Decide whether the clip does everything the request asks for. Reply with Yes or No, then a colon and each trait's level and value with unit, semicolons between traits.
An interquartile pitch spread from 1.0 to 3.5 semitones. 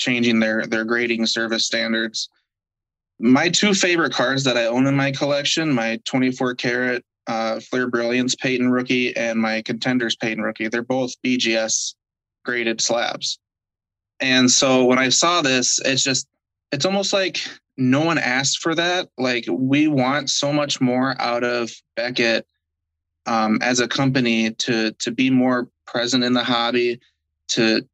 Yes: average, 2.8 semitones